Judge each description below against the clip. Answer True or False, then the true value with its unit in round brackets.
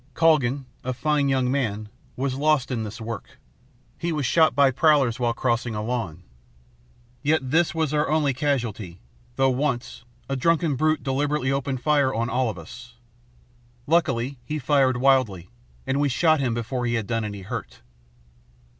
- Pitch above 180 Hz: False (130 Hz)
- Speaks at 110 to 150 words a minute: False (165 wpm)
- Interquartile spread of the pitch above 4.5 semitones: False (3.7 semitones)